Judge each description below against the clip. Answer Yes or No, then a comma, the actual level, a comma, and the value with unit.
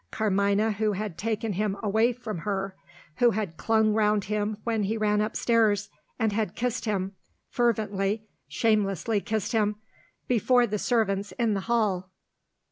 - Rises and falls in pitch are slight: Yes, narrow, 1.9 semitones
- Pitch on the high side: Yes, high, 215 Hz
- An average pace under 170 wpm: Yes, average, 145 wpm